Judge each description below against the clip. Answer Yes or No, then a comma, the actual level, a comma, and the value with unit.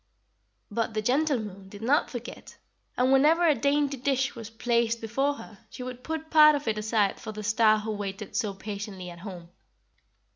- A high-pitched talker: Yes, high, 230 Hz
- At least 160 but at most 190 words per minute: Yes, average, 185 wpm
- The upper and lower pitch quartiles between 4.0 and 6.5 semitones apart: Yes, average, 4.4 semitones